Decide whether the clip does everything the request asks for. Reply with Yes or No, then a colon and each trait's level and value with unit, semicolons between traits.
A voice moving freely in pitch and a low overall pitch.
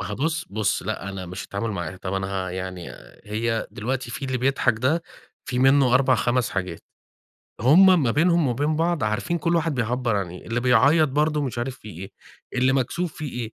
Yes: wide, 5.8 semitones; low, 125 Hz